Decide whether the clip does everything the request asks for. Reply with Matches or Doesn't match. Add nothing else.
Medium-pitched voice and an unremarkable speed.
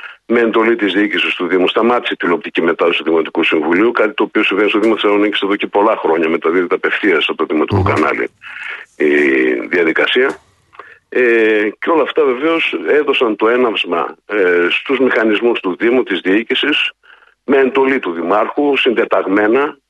Matches